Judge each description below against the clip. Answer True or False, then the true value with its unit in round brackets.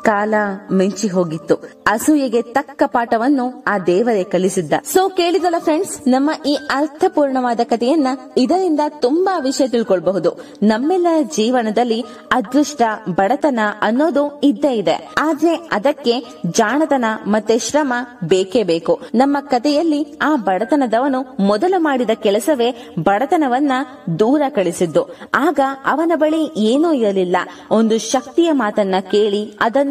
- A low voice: False (250 Hz)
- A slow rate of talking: True (110 wpm)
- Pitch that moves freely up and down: True (5.8 semitones)